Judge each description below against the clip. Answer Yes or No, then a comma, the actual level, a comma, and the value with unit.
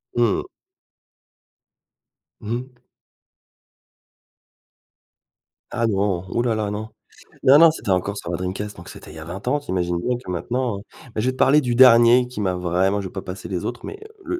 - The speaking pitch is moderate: No, low, 110 Hz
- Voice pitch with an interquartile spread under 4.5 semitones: No, average, 5.0 semitones